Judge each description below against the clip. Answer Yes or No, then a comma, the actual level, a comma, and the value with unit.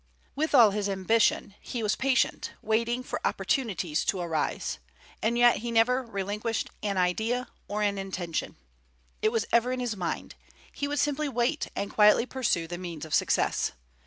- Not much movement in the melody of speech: No, average, 4.1 semitones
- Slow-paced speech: No, average, 165 wpm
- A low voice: No, high, 220 Hz